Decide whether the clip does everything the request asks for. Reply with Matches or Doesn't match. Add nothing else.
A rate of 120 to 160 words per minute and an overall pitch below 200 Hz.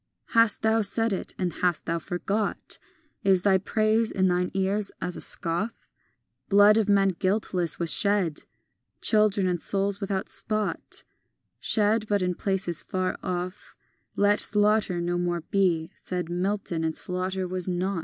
Matches